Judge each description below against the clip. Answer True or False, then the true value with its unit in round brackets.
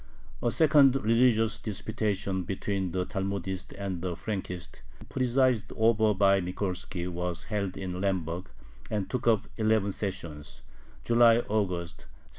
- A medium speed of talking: False (125 wpm)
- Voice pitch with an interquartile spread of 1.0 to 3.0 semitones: False (3.4 semitones)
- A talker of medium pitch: False (100 Hz)